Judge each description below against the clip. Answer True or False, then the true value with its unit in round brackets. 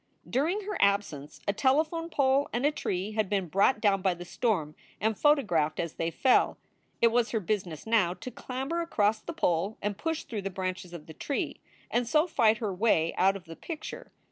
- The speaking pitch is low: False (215 Hz)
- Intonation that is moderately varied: False (6.4 semitones)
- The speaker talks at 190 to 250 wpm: True (200 wpm)